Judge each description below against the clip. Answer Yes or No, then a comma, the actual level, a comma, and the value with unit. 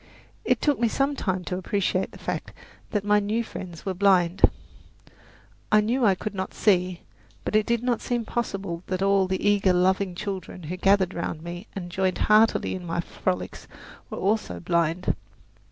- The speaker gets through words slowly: No, average, 175 wpm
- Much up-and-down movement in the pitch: No, average, 2.8 semitones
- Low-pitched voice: No, high, 190 Hz